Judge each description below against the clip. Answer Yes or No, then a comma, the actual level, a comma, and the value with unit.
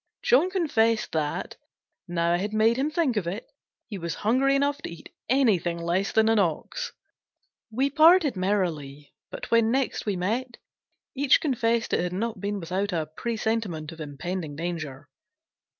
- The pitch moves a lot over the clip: Yes, wide, 6.6 semitones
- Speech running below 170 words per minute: Yes, average, 160 wpm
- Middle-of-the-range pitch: No, high, 210 Hz